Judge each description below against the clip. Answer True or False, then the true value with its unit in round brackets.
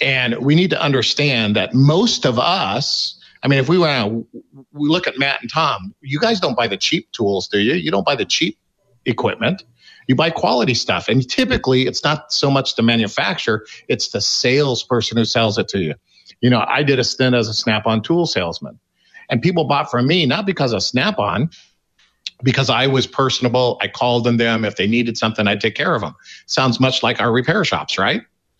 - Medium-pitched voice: False (130 Hz)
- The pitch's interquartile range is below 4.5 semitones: True (3.8 semitones)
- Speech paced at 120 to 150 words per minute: False (205 wpm)